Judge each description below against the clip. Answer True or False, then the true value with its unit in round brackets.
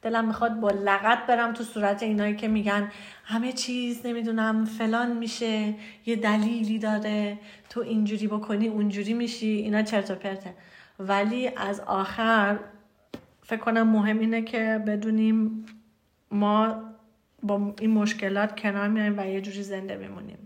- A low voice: False (215 Hz)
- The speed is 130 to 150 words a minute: True (140 wpm)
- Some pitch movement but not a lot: False (1.6 semitones)